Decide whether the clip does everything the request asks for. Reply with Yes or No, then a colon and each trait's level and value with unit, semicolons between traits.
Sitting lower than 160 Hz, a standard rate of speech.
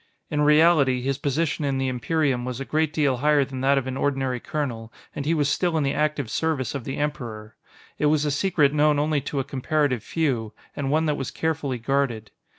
No: medium, 140 Hz; fast, 215 wpm